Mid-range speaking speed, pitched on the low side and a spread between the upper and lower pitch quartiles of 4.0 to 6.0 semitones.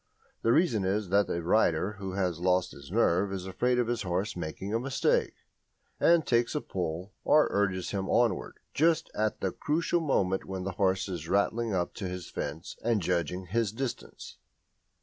Yes: average, 180 wpm; very low, 95 Hz; average, 4.3 semitones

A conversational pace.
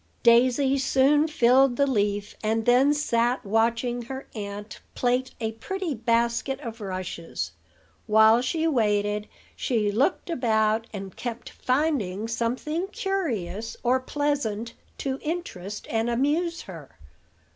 No: slow, 120 wpm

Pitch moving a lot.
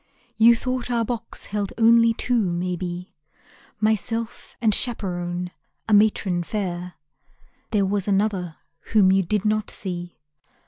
No: average, 3.8 semitones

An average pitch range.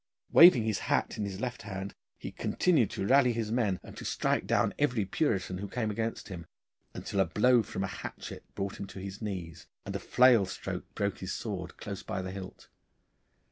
Yes: average, 3.5 semitones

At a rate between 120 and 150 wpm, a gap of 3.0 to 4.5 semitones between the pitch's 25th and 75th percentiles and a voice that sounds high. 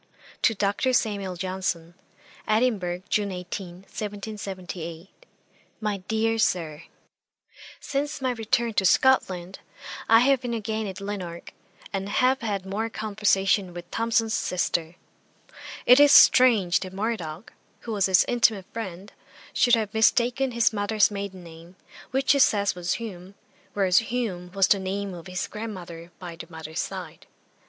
Yes: average, 140 wpm; average, 3.7 semitones; high, 200 Hz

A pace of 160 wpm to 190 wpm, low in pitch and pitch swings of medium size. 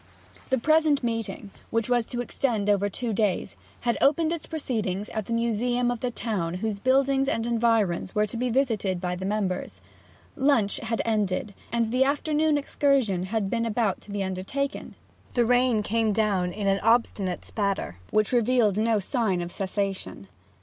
No: average, 170 wpm; high, 225 Hz; average, 3.7 semitones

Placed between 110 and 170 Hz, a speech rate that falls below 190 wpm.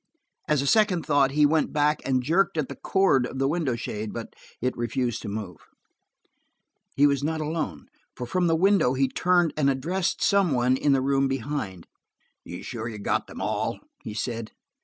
No: low, 135 Hz; average, 200 wpm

